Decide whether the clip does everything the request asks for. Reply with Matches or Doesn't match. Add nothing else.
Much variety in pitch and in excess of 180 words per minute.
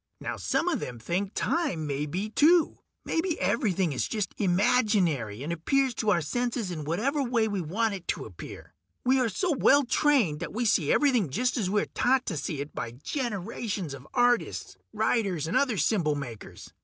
Matches